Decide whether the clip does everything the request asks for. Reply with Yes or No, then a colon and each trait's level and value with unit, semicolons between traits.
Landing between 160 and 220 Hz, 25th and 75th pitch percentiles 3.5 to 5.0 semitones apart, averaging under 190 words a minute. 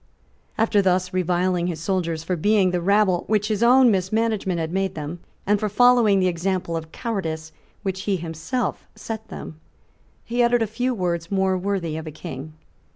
Yes: medium, 185 Hz; average, 3.8 semitones; average, 180 wpm